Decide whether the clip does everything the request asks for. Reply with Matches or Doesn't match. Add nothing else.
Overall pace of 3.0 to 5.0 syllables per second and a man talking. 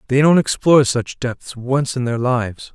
Matches